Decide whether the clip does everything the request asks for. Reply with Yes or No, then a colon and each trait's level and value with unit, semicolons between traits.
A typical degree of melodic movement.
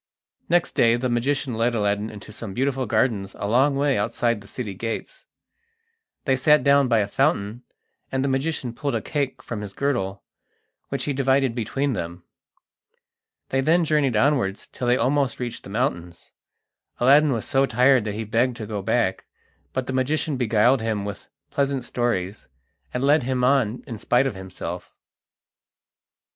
Yes: average, 4.2 semitones